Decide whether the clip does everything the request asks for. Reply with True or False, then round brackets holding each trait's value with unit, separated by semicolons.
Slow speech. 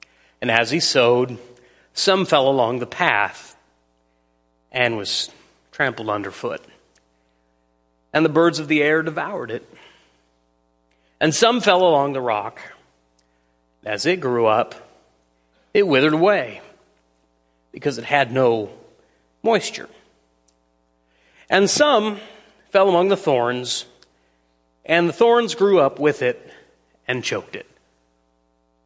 True (115 wpm)